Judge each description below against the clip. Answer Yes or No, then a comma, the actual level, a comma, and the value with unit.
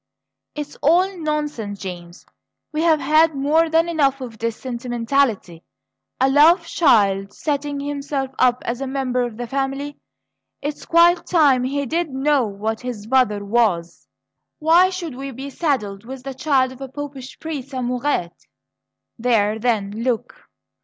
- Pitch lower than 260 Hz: No, very high, 270 Hz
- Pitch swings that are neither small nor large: Yes, average, 4.1 semitones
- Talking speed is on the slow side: No, average, 145 wpm